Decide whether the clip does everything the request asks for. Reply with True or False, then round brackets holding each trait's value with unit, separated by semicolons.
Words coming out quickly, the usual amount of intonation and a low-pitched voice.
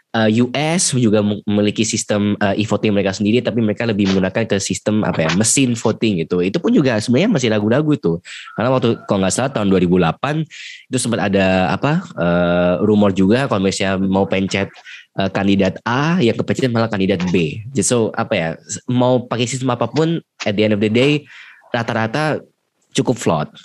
True (170 wpm; 3.8 semitones; 105 Hz)